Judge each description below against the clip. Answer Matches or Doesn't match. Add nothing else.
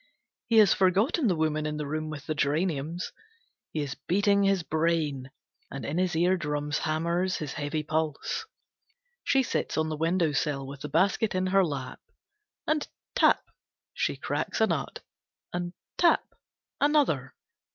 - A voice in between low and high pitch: Matches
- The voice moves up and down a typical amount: Matches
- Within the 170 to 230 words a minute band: Doesn't match